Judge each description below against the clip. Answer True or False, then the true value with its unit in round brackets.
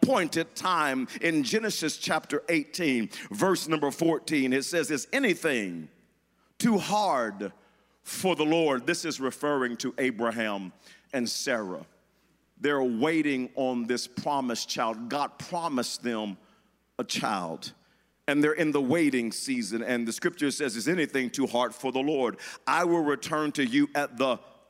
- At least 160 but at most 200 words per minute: False (145 wpm)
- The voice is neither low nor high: True (145 Hz)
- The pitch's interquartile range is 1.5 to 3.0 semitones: False (4.9 semitones)